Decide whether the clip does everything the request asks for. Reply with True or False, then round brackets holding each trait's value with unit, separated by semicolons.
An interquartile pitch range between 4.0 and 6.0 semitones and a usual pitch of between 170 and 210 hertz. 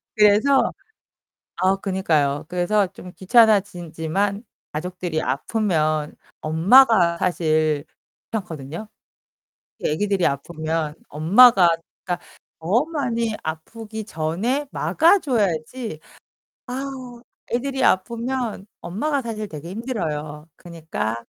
False (6.5 semitones; 190 Hz)